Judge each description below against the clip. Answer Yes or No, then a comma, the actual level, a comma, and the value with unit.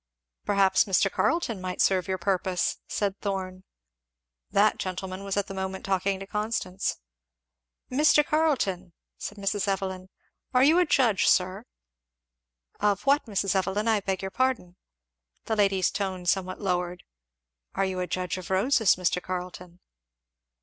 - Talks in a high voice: Yes, high, 195 Hz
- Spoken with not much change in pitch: Yes, narrow, 2.0 semitones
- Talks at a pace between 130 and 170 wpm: Yes, average, 145 wpm